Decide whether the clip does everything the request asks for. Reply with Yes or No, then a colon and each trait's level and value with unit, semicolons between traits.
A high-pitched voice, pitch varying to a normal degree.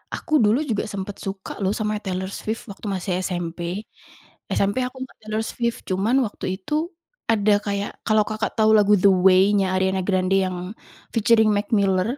No: high, 200 Hz; narrow, 2.3 semitones